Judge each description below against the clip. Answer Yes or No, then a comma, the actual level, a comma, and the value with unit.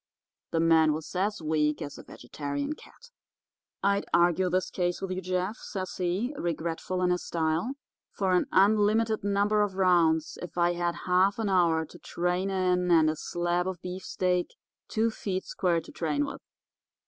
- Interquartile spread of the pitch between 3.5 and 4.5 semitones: No, narrow, 2.6 semitones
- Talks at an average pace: Yes, average, 170 wpm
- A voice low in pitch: No, medium, 180 Hz